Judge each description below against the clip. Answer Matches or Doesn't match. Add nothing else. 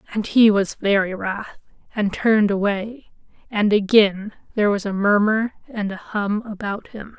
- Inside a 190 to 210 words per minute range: Doesn't match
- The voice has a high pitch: Matches